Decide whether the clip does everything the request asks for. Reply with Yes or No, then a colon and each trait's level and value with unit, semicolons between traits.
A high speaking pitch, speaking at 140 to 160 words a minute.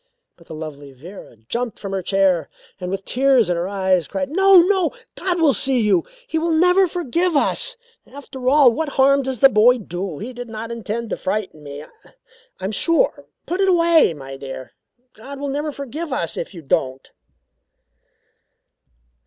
No: high, 235 Hz; average, 180 wpm